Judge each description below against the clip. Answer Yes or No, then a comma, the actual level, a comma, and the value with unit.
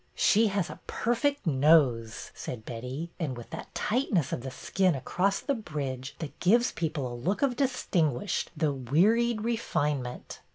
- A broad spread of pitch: Yes, wide, 8.6 semitones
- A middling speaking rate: Yes, average, 170 wpm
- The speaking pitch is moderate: Yes, medium, 165 Hz